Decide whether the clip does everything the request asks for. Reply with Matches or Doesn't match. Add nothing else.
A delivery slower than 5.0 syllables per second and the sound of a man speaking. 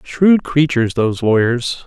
Matches